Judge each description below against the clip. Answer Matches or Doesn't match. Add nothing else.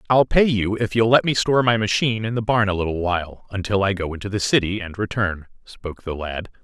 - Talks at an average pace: Doesn't match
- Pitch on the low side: Matches